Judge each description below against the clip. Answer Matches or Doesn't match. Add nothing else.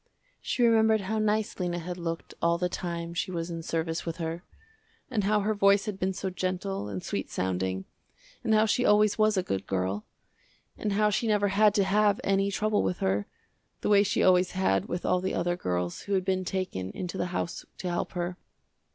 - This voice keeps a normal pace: Doesn't match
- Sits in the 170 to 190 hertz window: Matches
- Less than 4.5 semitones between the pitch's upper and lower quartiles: Matches